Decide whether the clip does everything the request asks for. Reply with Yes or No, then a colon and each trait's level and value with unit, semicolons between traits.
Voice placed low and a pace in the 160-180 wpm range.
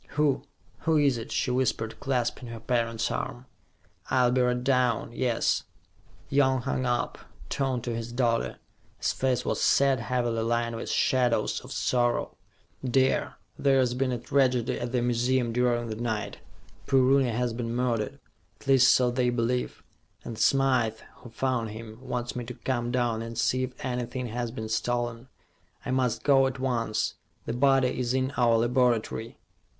Yes: low, 125 Hz; average, 165 wpm